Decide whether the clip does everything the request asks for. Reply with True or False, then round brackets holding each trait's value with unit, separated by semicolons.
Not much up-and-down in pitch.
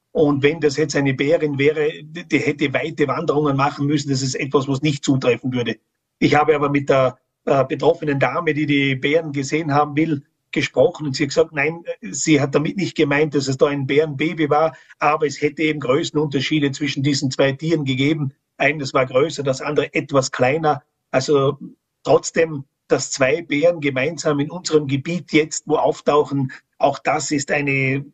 True (1.8 semitones)